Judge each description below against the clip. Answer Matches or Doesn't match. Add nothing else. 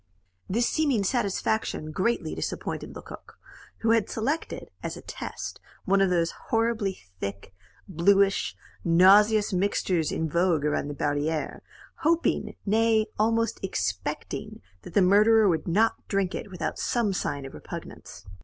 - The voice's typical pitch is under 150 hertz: Doesn't match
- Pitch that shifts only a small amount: Doesn't match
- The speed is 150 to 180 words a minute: Doesn't match